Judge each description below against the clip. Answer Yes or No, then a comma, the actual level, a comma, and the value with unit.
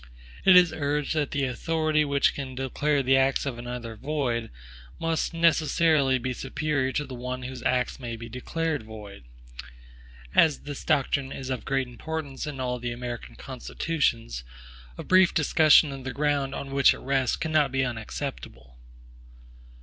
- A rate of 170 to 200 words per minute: No, average, 155 wpm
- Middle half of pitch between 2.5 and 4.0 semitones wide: Yes, average, 3.2 semitones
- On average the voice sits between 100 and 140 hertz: Yes, low, 135 Hz